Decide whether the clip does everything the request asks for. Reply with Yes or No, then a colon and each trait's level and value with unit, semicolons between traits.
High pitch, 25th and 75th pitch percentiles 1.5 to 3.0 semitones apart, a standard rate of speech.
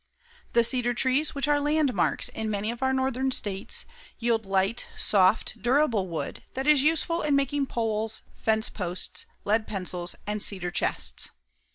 No: high, 230 Hz; average, 4.8 semitones; average, 155 wpm